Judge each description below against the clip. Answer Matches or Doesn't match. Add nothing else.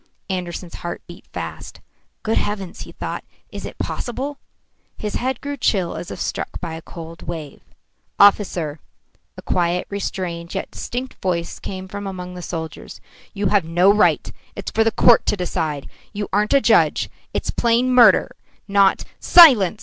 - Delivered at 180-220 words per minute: Doesn't match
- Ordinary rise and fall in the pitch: Matches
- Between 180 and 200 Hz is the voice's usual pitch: Matches